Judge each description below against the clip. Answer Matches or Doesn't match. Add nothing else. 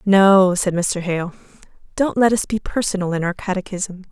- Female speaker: Matches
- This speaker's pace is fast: Doesn't match